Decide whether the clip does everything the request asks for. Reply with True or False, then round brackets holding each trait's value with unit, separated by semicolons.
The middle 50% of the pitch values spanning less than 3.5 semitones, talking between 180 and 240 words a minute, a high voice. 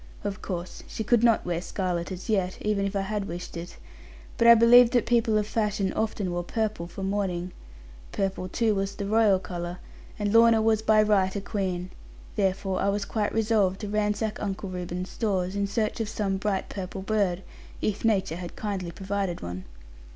True (2.6 semitones; 190 wpm; 200 Hz)